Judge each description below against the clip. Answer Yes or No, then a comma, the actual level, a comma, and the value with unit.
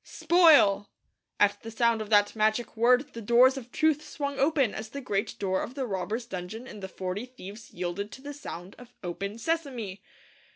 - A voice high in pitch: Yes, high, 230 Hz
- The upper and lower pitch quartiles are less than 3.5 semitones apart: No, average, 4.7 semitones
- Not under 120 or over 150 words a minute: No, average, 190 wpm